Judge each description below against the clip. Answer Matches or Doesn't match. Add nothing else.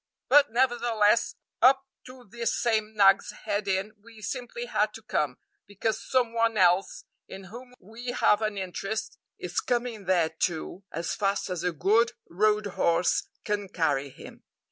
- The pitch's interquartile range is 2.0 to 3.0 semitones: Doesn't match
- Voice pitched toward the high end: Matches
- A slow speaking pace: Doesn't match